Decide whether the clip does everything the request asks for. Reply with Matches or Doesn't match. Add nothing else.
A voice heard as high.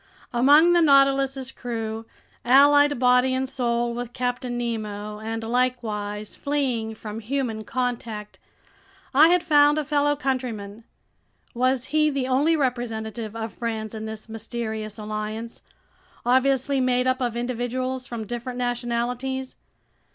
Matches